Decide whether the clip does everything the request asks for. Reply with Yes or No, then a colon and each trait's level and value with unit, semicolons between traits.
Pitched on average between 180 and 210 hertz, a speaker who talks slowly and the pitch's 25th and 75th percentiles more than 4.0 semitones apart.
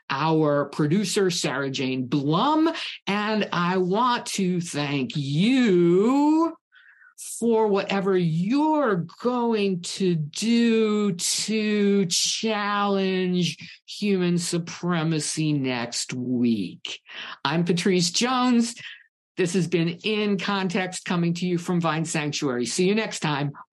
Yes: medium, 185 Hz; slow, 105 wpm; average, 4.6 semitones